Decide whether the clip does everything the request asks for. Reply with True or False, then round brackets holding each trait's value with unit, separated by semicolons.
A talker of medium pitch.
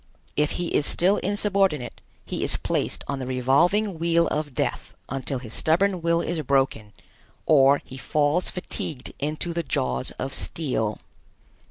True (150 Hz)